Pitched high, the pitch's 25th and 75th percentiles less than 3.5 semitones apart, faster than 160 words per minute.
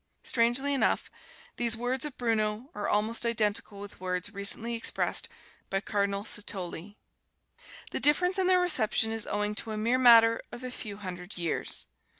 No: high, 220 Hz; average, 3.0 semitones; average, 155 wpm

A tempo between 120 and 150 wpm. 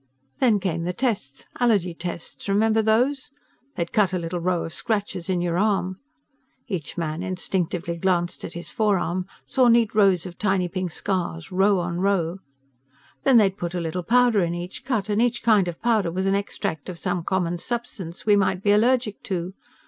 No: average, 185 wpm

